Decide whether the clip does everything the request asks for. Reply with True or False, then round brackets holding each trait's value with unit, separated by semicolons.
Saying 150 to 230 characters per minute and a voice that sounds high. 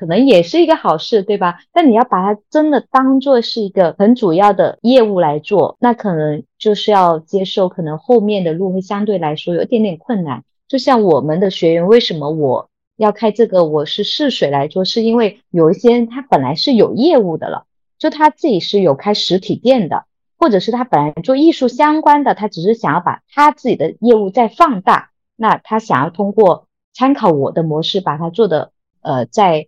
False (295 characters per minute; 210 Hz)